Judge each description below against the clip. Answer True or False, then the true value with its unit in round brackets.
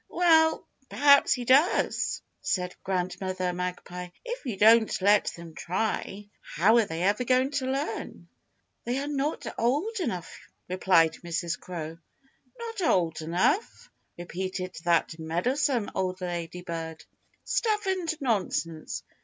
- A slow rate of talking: True (125 wpm)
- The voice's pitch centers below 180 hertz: False (190 Hz)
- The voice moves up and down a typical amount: False (7.7 semitones)